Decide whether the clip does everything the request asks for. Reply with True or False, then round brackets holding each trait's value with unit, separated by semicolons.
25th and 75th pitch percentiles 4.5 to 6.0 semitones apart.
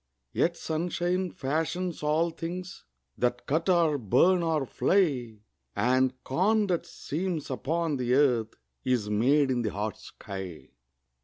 True (5.6 semitones)